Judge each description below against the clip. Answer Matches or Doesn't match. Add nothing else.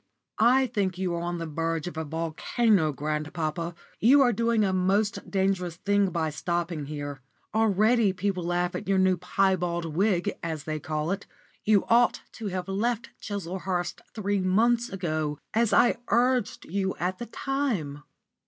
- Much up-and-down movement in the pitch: Doesn't match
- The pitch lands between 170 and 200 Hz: Matches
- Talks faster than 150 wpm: Matches